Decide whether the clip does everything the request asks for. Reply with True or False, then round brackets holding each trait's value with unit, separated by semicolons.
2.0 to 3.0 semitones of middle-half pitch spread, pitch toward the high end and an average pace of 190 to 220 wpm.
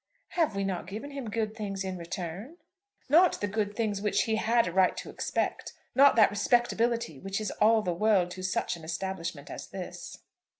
False (3.5 semitones; 205 Hz; 195 wpm)